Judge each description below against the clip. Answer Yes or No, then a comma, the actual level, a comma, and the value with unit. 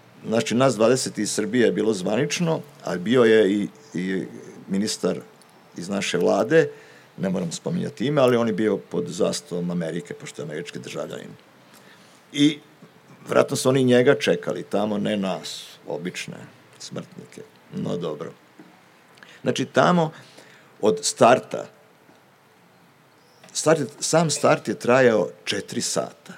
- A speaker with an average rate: Yes, average, 125 wpm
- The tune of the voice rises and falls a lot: Yes, wide, 6.3 semitones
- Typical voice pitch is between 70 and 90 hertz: No, low, 130 Hz